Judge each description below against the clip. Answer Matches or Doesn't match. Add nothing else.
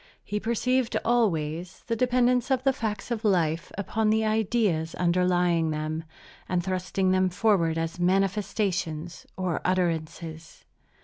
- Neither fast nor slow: Doesn't match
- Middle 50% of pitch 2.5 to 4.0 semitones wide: Doesn't match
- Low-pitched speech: Doesn't match